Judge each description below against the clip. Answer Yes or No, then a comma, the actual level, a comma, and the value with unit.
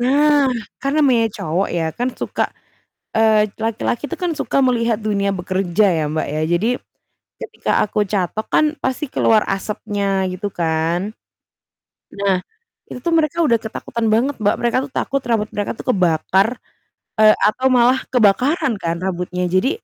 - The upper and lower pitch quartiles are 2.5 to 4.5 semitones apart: No, average, 5.1 semitones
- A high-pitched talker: Yes, high, 215 Hz